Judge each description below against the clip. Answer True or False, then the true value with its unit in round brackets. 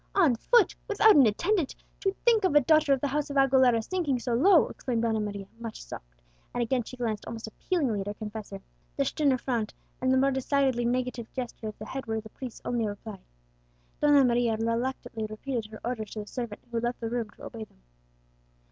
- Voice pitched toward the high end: True (240 Hz)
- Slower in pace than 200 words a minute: False (205 wpm)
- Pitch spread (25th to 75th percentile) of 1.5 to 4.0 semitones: True (3.7 semitones)